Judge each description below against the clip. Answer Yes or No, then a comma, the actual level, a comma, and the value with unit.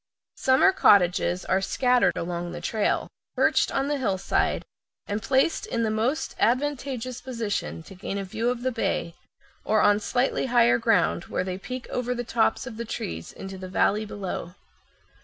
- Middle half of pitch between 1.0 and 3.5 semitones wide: No, average, 4.7 semitones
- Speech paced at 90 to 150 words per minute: No, average, 170 wpm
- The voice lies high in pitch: Yes, high, 225 Hz